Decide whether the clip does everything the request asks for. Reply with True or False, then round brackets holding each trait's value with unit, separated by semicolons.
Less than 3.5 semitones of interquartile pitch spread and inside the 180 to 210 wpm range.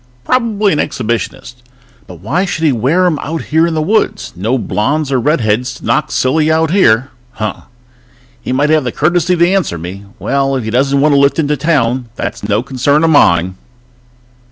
False (4.7 semitones; 190 wpm)